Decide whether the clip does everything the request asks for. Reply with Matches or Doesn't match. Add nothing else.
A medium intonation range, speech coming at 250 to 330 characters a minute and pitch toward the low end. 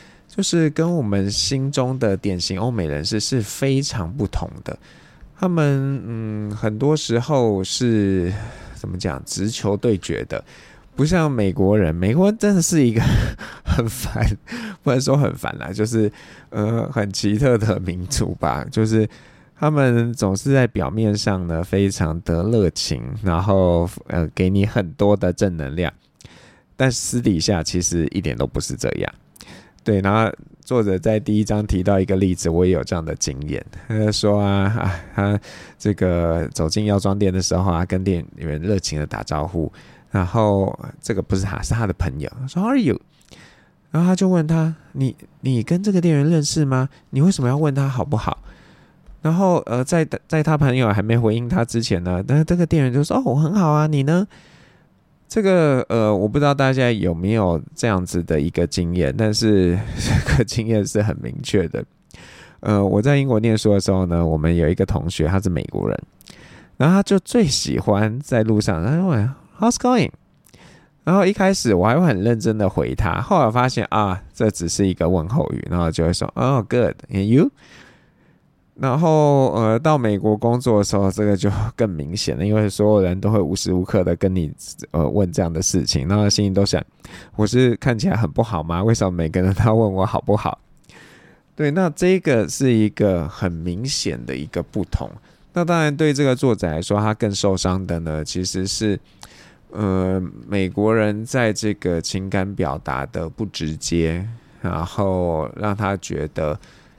Doesn't match